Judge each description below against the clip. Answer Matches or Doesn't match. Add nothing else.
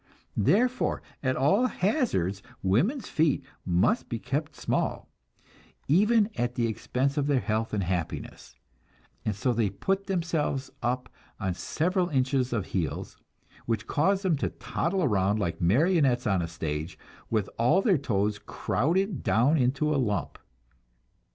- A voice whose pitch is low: Matches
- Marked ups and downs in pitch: Matches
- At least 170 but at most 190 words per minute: Doesn't match